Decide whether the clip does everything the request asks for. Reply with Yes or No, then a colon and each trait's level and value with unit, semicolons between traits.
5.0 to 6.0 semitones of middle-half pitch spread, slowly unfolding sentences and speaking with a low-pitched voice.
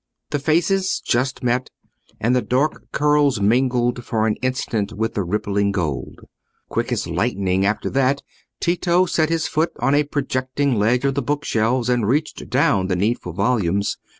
No: average, 5.3 semitones; average, 165 wpm; low, 125 Hz